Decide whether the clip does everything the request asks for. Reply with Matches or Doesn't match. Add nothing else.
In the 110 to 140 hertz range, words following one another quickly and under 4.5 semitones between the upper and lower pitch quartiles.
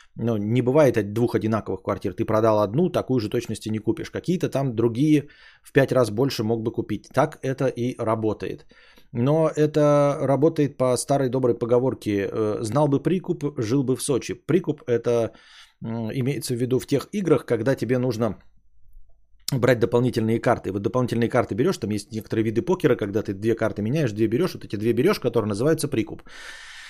Matches